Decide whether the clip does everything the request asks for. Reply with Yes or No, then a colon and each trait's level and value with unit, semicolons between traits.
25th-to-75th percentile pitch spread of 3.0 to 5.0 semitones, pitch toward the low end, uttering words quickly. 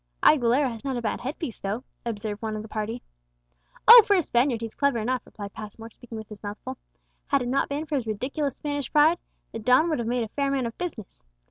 No: average, 4.2 semitones; high, 245 Hz; fast, 240 wpm